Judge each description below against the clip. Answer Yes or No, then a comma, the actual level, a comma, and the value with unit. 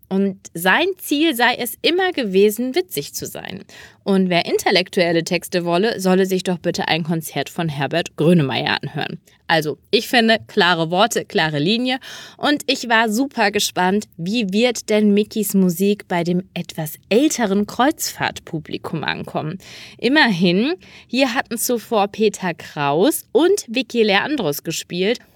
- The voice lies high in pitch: Yes, high, 205 Hz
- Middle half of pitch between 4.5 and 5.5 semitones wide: Yes, average, 5.2 semitones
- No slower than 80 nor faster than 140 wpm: Yes, average, 135 wpm